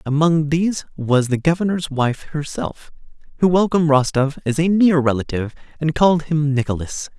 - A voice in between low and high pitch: Yes, medium, 150 Hz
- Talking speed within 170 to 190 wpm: No, average, 150 wpm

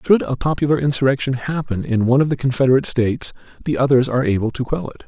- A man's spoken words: Yes, male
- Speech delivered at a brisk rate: Yes, fast, 215 wpm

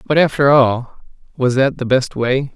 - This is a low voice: Yes, low, 130 Hz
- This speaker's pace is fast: No, average, 190 wpm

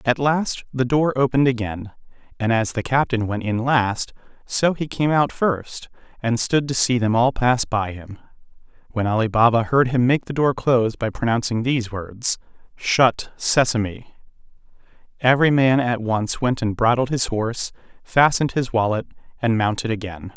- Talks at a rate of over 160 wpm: Yes, average, 170 wpm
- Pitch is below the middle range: Yes, low, 120 Hz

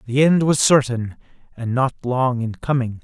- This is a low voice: Yes, low, 130 Hz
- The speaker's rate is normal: Yes, average, 180 wpm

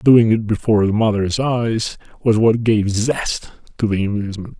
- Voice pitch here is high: No, low, 110 Hz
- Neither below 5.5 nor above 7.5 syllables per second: No, 4.6 syllables/s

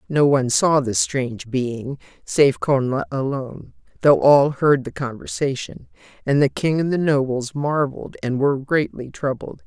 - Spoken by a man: No, female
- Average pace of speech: Yes, average, 155 wpm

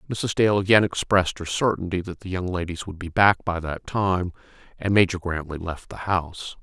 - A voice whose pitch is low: Yes, very low, 90 Hz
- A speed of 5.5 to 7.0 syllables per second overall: No, 5.3 syllables/s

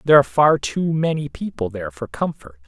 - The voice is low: Yes, low, 130 Hz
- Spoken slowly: No, average, 200 wpm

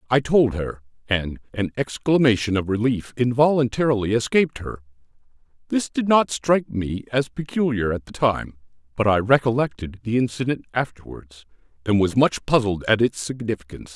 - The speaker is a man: Yes, male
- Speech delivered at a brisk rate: No, average, 145 wpm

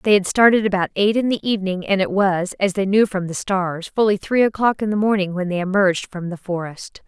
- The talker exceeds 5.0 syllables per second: Yes, 5.7 syllables/s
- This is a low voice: No, high, 195 Hz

